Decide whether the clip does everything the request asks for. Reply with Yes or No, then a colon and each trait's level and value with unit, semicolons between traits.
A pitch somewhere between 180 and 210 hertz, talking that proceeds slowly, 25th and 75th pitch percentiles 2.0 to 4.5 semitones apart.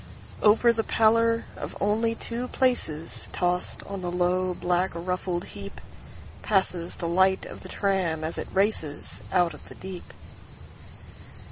Yes: high, 190 Hz; slow, 125 wpm; average, 3.4 semitones